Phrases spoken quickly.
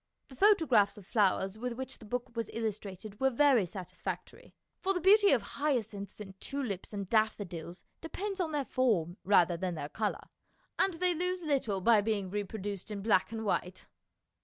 No: average, 180 wpm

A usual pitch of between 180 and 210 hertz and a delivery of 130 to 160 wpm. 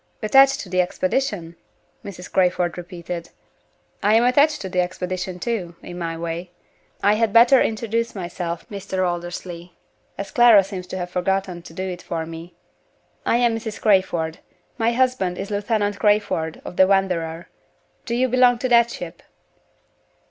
Yes: high, 190 Hz; average, 155 wpm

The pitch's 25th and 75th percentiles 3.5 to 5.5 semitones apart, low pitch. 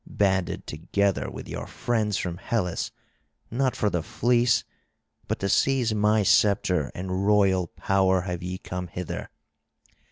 No: average, 2.8 semitones; very low, 95 Hz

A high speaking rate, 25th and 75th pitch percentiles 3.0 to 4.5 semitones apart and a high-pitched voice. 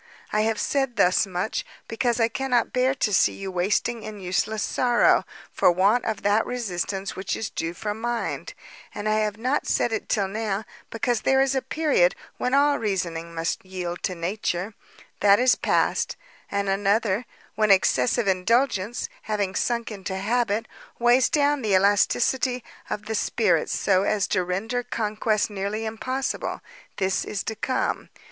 No: average, 160 wpm; average, 3.8 semitones; high, 215 Hz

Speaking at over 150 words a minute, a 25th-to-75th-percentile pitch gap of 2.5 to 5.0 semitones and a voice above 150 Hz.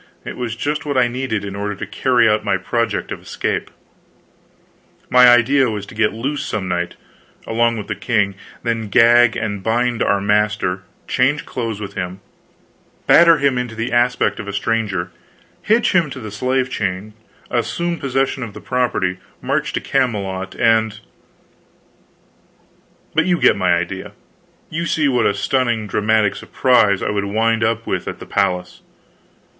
No: average, 160 wpm; average, 3.8 semitones; low, 115 Hz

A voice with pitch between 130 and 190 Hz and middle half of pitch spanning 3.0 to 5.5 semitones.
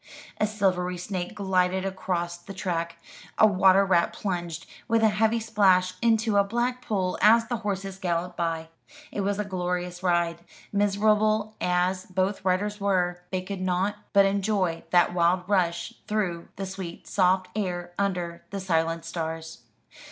No: medium, 185 Hz; narrow, 2.4 semitones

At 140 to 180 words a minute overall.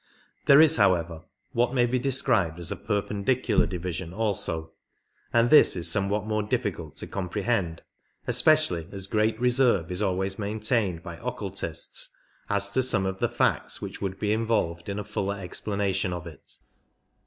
Yes: average, 165 wpm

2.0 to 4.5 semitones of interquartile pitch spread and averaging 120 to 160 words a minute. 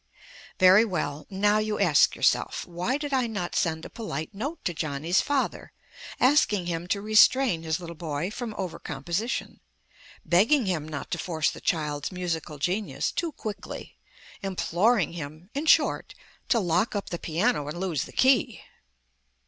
No: average, 5.2 semitones; average, 155 wpm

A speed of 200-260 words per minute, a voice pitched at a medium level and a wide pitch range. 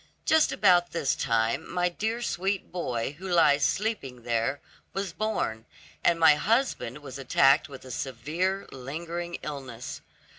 No: average, 140 wpm; medium, 155 Hz; wide, 5.9 semitones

